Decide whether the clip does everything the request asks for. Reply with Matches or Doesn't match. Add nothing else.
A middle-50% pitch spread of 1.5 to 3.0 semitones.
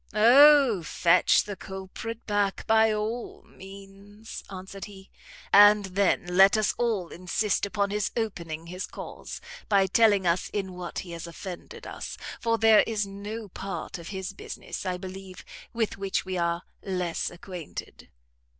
Matches